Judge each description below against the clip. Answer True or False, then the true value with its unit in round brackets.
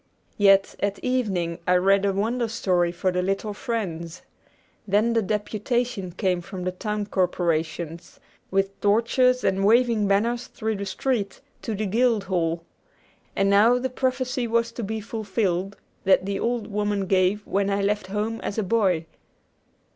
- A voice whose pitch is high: True (200 Hz)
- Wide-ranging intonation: False (3.3 semitones)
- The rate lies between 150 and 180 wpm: True (155 wpm)